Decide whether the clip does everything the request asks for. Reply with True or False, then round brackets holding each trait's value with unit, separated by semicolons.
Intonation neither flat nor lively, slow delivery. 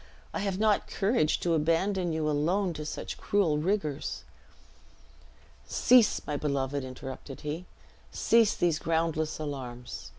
True (4.7 semitones; 125 wpm)